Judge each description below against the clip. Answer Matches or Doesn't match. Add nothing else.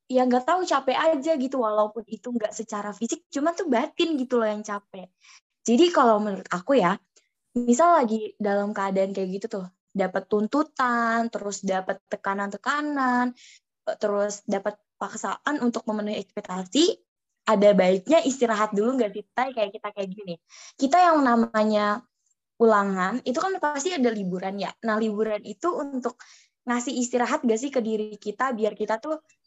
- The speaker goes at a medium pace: Doesn't match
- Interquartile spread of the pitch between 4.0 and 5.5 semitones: Matches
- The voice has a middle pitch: Doesn't match